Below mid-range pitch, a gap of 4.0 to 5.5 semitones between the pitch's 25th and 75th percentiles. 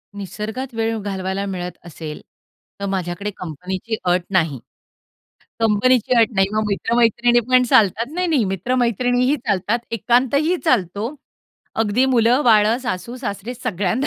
No: high, 220 Hz; average, 4.3 semitones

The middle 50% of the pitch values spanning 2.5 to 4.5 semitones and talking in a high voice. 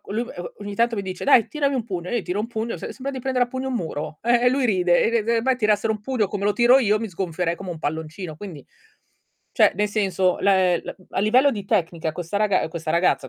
No: average, 5.0 semitones; high, 205 Hz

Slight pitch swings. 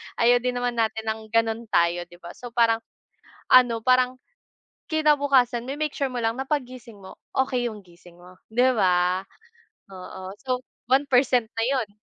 No: average, 3.8 semitones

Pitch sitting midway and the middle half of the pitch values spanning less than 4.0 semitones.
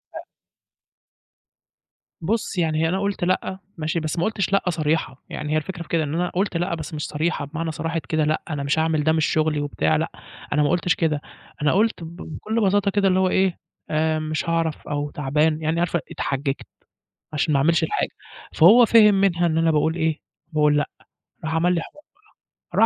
Yes: medium, 160 Hz; average, 2.7 semitones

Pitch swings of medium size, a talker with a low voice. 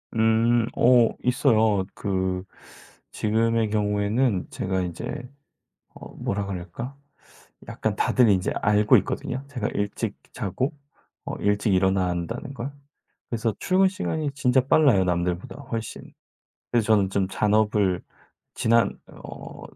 Yes: average, 4.1 semitones; low, 110 Hz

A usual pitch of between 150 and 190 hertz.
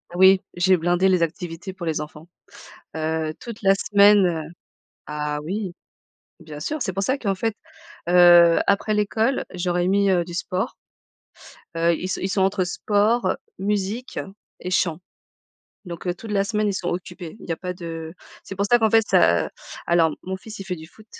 Yes: medium, 185 Hz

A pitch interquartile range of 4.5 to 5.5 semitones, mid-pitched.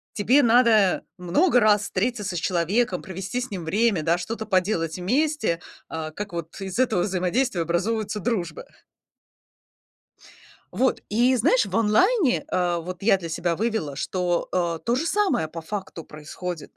No: average, 5.2 semitones; high, 195 Hz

